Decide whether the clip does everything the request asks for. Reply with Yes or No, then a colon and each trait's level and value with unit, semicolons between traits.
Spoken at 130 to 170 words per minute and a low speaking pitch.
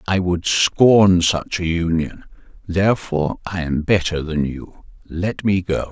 Yes: average, 140 wpm; very low, 90 Hz